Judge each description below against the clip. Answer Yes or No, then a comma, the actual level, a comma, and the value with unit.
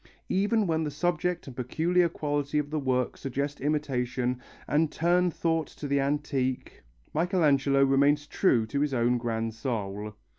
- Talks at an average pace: Yes, average, 150 wpm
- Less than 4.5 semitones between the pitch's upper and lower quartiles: Yes, average, 4.0 semitones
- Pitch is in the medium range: Yes, medium, 145 Hz